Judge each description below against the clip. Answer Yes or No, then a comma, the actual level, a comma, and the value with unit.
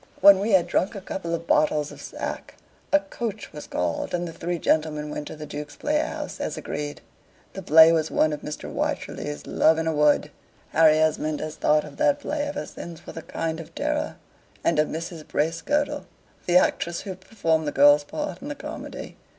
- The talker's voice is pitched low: No, medium, 160 Hz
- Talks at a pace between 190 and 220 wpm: Yes, average, 200 wpm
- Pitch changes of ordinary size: Yes, average, 4.0 semitones